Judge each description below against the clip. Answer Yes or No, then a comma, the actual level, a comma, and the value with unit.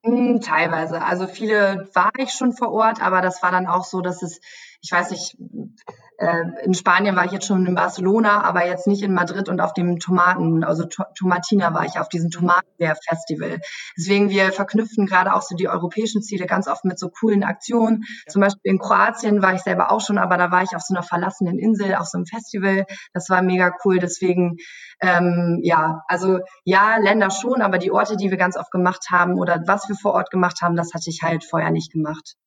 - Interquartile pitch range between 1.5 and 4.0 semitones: Yes, narrow, 2.4 semitones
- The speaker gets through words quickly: Yes, fast, 215 wpm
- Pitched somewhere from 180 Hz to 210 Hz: Yes, medium, 185 Hz